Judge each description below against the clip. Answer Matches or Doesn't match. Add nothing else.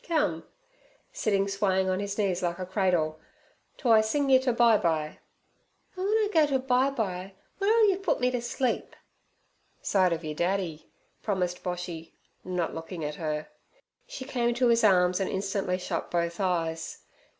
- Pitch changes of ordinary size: Doesn't match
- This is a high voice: Matches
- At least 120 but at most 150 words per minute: Doesn't match